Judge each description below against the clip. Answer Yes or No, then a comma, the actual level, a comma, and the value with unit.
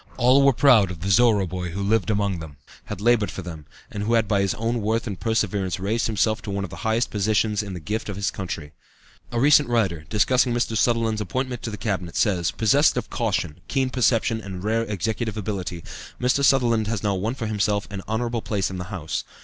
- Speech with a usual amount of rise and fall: Yes, average, 3.1 semitones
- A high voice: No, low, 105 Hz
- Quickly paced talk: Yes, fast, 220 wpm